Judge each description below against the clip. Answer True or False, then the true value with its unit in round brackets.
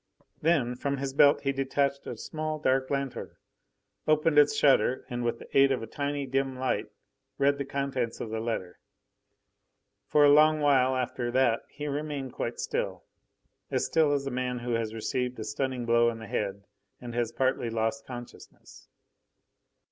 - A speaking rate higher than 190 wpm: False (170 wpm)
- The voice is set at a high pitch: False (130 Hz)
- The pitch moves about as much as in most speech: True (3.0 semitones)